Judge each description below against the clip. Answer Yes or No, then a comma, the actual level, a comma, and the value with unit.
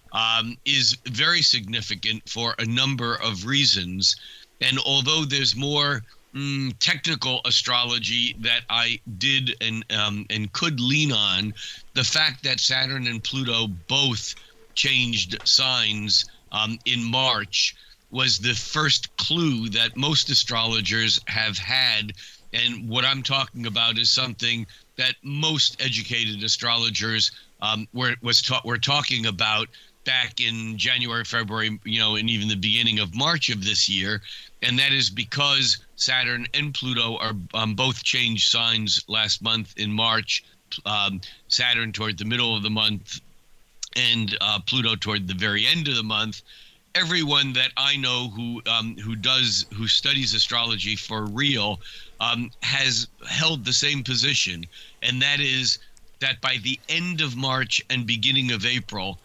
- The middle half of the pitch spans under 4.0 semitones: Yes, average, 3.2 semitones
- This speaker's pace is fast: No, average, 145 wpm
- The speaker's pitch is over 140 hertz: No, low, 120 Hz